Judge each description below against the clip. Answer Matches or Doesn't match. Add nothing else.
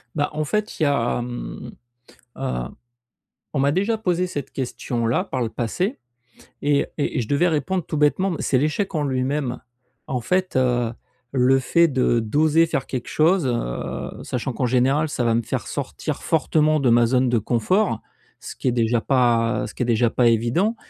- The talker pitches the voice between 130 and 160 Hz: Matches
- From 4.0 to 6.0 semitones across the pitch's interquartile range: Matches